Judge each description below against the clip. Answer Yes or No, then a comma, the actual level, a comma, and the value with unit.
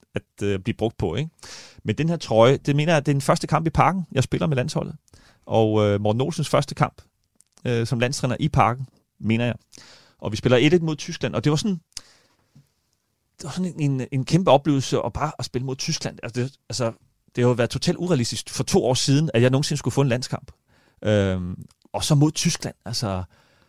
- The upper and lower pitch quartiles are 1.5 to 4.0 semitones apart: No, average, 4.6 semitones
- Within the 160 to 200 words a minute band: No, average, 220 wpm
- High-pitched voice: No, low, 135 Hz